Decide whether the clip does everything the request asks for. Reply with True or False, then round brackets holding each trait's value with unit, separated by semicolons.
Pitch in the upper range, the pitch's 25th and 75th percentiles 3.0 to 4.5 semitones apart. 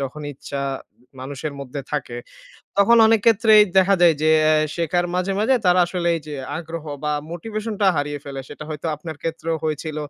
False (165 Hz; 4.2 semitones)